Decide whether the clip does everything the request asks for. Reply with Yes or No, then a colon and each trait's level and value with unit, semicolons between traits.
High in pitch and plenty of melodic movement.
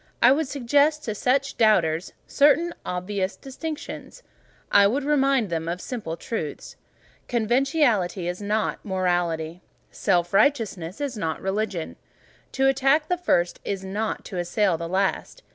Yes: high, 210 Hz; wide, 7.3 semitones